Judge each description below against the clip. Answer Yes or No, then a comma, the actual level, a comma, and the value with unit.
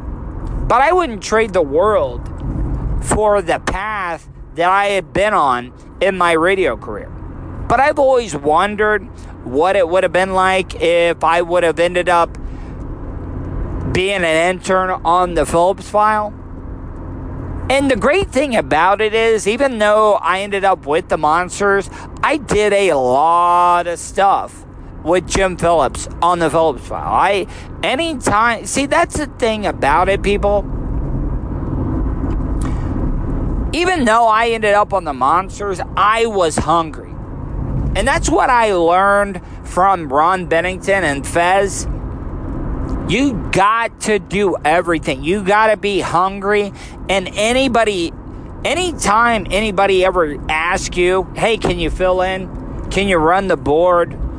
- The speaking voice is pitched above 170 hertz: Yes, medium, 185 Hz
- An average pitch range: Yes, average, 3.9 semitones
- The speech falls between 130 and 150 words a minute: Yes, average, 140 wpm